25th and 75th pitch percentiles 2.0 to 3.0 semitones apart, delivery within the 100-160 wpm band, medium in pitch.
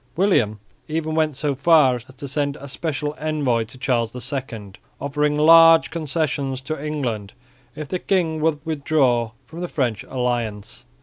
No: average, 3.9 semitones; average, 150 wpm; medium, 145 Hz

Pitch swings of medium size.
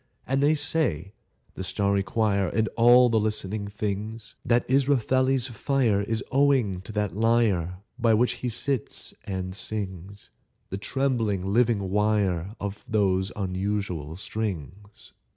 Yes: average, 3.3 semitones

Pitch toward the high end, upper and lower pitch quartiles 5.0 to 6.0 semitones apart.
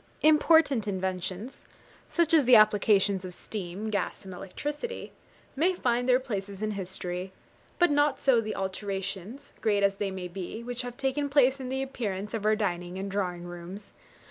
Yes: high, 210 Hz; wide, 5.4 semitones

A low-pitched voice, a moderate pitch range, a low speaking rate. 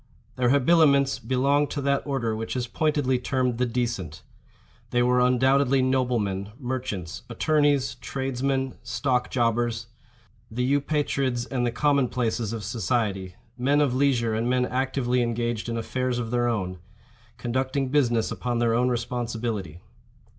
No: low, 125 Hz; narrow, 2.3 semitones; slow, 130 wpm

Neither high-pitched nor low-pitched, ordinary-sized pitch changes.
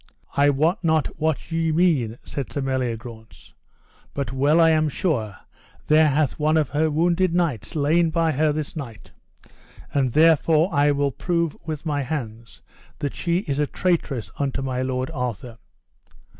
Yes: medium, 145 Hz; average, 3.6 semitones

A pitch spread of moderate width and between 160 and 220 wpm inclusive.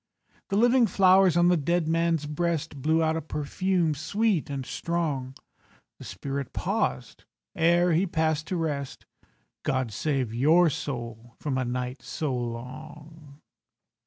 No: average, 4.2 semitones; slow, 135 wpm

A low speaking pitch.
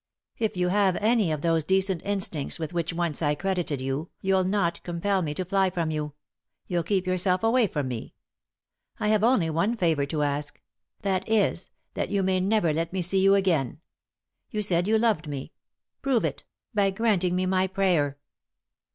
No: medium, 185 Hz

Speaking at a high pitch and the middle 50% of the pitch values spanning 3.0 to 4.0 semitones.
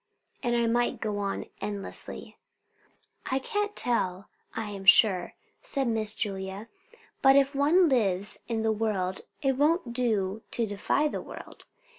No: high, 225 Hz; average, 4.9 semitones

